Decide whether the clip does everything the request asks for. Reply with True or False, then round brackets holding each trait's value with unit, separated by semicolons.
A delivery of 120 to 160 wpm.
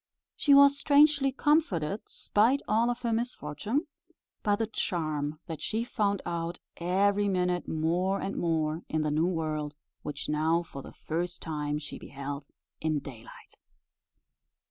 True (145 wpm)